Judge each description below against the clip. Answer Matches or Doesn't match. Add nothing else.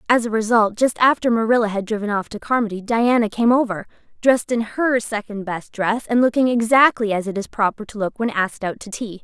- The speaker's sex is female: Matches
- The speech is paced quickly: Matches